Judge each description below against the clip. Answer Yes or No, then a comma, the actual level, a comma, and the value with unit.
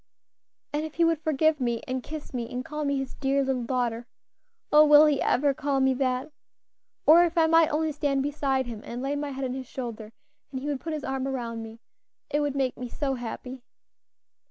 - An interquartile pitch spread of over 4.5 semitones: No, average, 2.8 semitones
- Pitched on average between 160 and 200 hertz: No, very high, 270 Hz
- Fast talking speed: Yes, fast, 215 wpm